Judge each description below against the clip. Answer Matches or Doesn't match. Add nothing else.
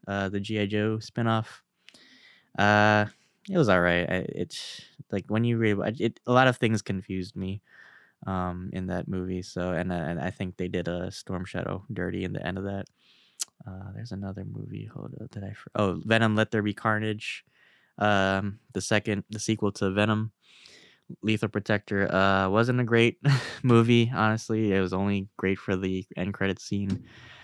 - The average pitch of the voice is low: Matches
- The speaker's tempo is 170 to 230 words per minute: Matches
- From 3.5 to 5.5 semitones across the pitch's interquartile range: Doesn't match